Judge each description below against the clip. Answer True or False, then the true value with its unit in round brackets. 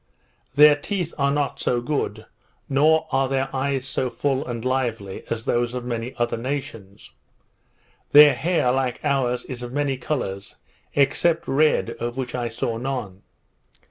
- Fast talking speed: False (150 wpm)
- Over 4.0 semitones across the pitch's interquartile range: False (3.0 semitones)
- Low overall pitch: True (130 Hz)